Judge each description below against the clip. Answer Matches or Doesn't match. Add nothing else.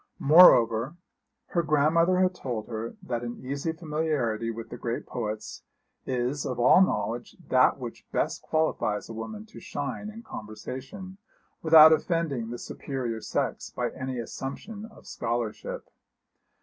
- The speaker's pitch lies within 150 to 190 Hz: Doesn't match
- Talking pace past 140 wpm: Doesn't match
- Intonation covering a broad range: Matches